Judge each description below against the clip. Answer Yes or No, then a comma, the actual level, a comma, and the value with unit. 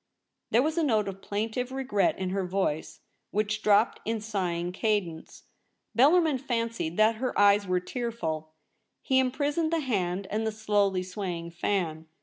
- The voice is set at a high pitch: Yes, high, 210 Hz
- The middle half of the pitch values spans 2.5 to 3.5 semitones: No, average, 4.7 semitones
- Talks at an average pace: Yes, average, 150 wpm